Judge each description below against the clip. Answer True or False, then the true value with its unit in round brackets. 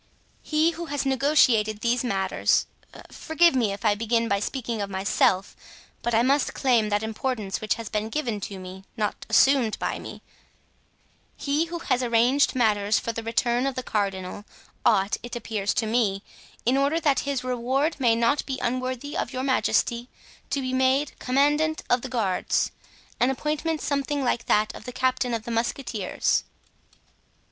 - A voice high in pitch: True (245 Hz)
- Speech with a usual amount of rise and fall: True (4.0 semitones)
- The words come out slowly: False (165 wpm)